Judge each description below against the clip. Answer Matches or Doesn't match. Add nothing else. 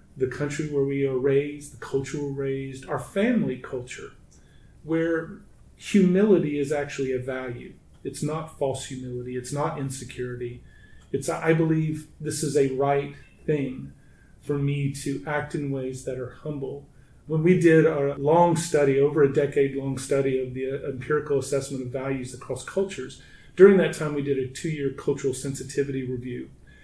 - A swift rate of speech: Doesn't match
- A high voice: Doesn't match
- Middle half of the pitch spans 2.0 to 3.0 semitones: Matches